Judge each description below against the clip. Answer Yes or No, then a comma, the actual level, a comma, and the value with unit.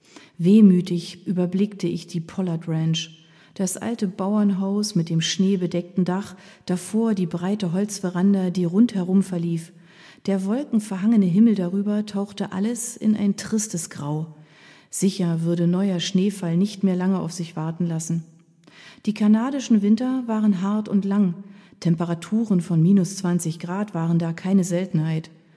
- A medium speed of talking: Yes, average, 135 wpm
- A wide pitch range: No, average, 2.8 semitones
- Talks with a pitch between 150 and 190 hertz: Yes, medium, 185 Hz